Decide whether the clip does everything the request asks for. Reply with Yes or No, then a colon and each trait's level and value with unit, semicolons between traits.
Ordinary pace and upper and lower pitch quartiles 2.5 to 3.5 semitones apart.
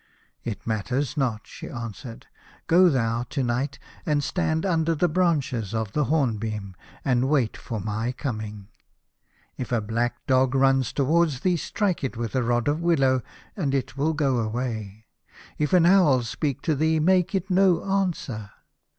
No: average, 165 wpm; wide, 5.5 semitones